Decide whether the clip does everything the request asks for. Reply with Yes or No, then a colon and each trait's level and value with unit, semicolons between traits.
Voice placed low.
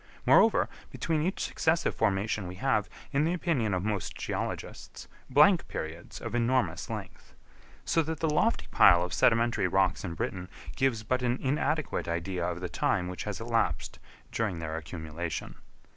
Yes: low, 110 Hz